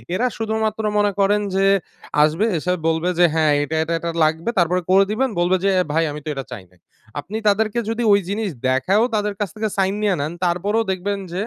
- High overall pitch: Yes, high, 195 Hz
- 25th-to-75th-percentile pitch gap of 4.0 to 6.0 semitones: Yes, average, 4.5 semitones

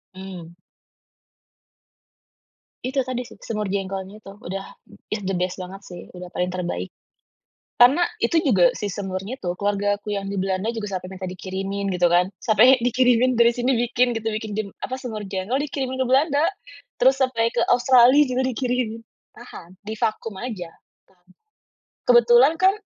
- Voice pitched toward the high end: Yes, high, 215 Hz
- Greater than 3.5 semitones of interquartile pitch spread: Yes, average, 4.7 semitones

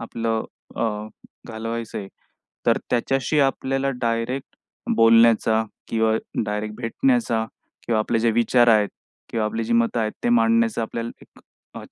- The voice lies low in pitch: Yes, low, 115 Hz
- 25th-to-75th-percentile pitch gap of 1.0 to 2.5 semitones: Yes, narrow, 2.0 semitones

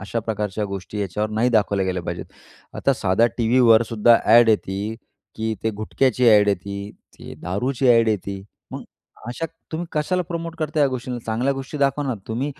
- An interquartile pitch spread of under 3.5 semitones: No, average, 4.3 semitones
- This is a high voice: No, low, 115 Hz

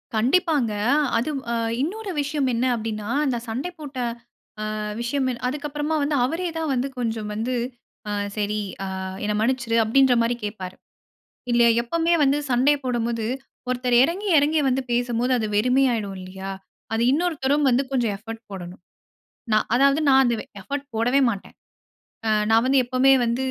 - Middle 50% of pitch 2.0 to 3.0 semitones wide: No, average, 3.9 semitones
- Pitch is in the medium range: No, very high, 250 Hz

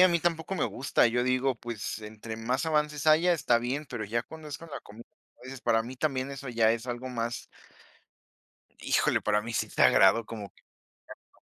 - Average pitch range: Yes, average, 4.6 semitones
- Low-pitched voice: Yes, low, 125 Hz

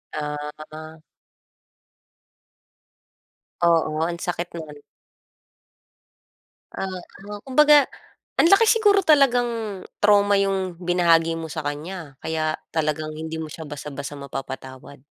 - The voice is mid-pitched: Yes, medium, 165 Hz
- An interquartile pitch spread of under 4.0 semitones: No, average, 4.7 semitones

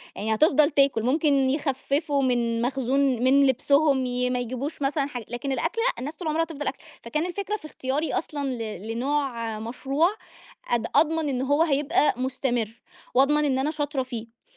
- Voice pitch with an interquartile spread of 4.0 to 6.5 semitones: No, average, 3.3 semitones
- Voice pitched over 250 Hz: Yes, very high, 275 Hz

